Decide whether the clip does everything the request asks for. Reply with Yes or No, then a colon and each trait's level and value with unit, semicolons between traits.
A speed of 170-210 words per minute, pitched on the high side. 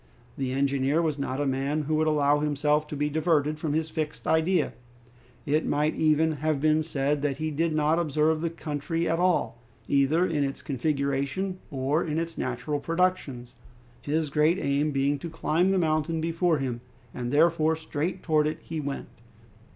No: average, 175 wpm; medium, 155 Hz